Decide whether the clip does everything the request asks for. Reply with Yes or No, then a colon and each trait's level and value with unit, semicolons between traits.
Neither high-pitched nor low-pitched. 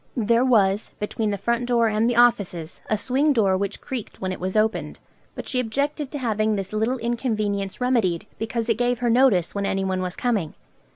No: high, 220 Hz